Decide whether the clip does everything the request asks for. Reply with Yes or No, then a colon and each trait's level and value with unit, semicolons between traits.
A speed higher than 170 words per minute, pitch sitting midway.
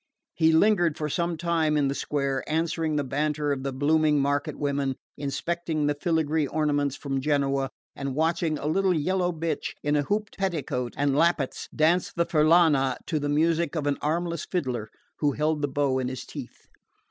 Yes: average, 180 wpm; medium, 150 Hz